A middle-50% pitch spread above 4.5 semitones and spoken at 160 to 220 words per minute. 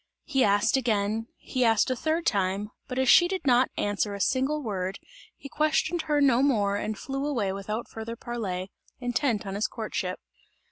Yes: average, 4.9 semitones; average, 180 wpm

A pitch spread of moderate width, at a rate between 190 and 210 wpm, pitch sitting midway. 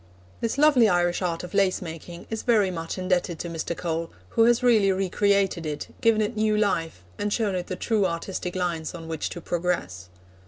Yes: average, 3.9 semitones; average, 200 wpm; medium, 180 Hz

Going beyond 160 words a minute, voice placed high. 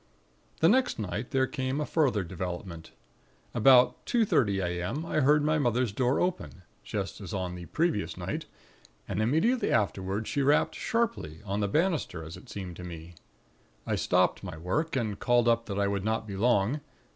No: average, 180 wpm; low, 110 Hz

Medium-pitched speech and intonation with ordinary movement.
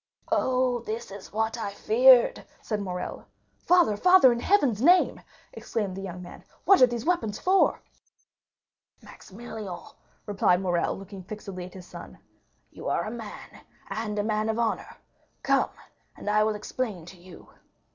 No: high, 215 Hz; average, 3.8 semitones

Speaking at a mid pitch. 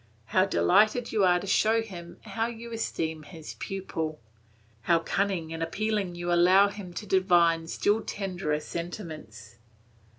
Yes: medium, 180 Hz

